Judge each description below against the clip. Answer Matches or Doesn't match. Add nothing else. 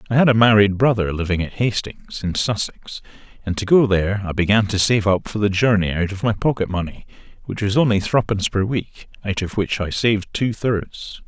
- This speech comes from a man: Matches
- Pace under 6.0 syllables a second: Matches